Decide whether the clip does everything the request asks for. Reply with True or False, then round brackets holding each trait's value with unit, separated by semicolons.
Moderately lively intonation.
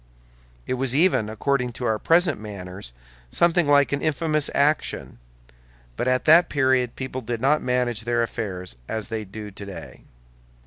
True (4.7 semitones)